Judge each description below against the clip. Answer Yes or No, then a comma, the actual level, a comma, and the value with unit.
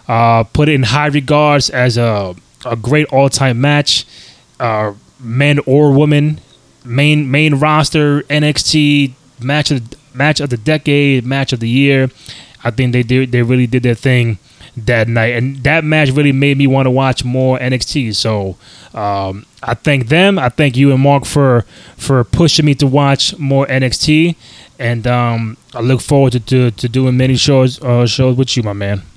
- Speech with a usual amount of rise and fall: Yes, average, 3.1 semitones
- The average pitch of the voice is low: Yes, low, 130 Hz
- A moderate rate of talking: Yes, average, 180 wpm